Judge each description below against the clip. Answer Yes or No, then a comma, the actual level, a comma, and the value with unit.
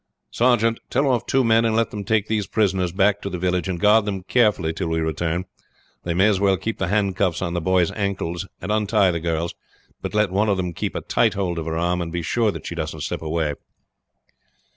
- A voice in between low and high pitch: No, very low, 95 Hz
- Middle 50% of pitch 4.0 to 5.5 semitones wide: No, average, 3.6 semitones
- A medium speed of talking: No, fast, 230 wpm